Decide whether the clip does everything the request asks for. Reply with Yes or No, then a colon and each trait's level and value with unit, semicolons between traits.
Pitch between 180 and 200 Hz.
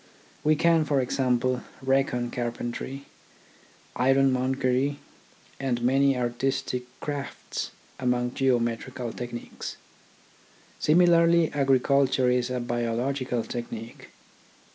No: low, 130 Hz